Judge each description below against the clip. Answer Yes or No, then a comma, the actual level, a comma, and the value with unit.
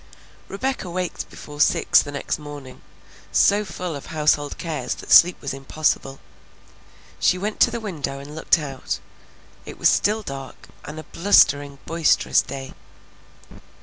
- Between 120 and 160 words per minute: Yes, average, 145 wpm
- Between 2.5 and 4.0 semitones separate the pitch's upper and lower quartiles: No, average, 4.6 semitones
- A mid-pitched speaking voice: Yes, medium, 150 Hz